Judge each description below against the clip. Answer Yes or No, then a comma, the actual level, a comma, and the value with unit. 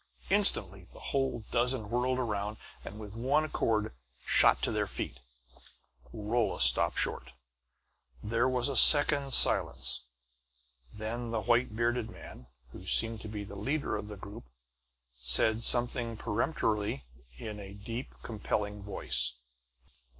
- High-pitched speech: No, low, 110 Hz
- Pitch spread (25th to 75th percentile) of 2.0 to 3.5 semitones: Yes, average, 2.9 semitones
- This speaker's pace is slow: Yes, slow, 130 wpm